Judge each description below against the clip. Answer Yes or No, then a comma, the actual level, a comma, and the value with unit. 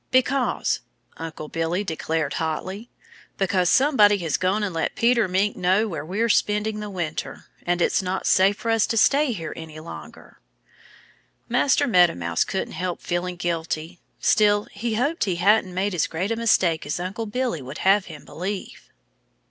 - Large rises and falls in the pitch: No, average, 4.2 semitones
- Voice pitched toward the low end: No, high, 190 Hz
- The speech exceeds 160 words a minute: Yes, average, 170 wpm